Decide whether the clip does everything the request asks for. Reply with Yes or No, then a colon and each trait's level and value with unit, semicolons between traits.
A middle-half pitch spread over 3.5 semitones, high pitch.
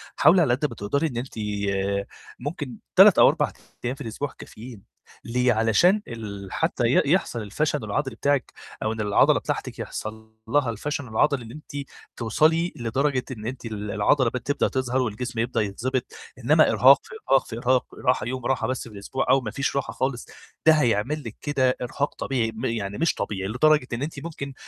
No: average, 4.1 semitones; low, 125 Hz